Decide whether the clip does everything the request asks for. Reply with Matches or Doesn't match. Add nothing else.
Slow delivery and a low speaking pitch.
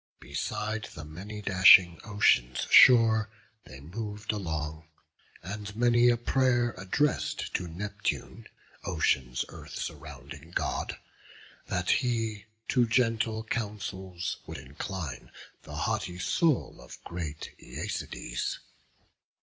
Matches